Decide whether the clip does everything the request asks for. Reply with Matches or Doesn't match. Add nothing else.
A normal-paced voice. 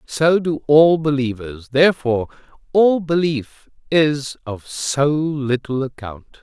Doesn't match